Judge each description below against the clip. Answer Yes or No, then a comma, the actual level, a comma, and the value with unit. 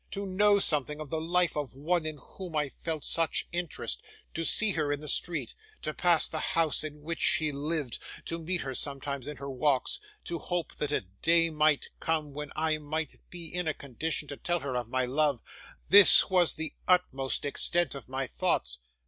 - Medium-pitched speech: Yes, medium, 155 Hz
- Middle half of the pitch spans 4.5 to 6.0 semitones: No, average, 3.0 semitones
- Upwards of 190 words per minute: Yes, average, 200 wpm